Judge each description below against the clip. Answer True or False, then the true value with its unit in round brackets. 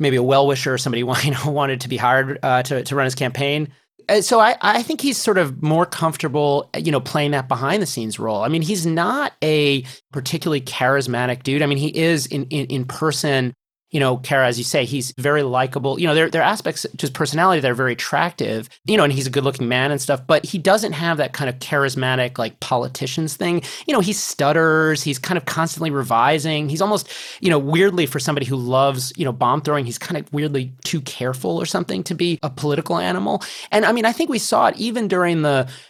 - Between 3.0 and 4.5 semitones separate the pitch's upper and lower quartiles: True (3.9 semitones)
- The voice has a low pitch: False (145 Hz)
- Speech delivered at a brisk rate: True (235 wpm)